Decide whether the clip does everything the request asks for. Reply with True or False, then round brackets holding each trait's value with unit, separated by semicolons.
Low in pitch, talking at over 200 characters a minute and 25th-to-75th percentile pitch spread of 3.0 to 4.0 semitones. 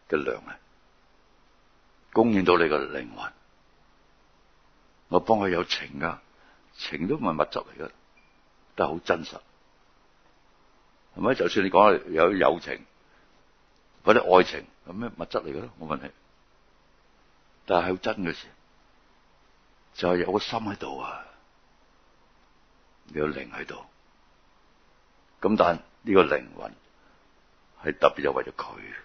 False (90 Hz; 170 characters per minute; 3.4 semitones)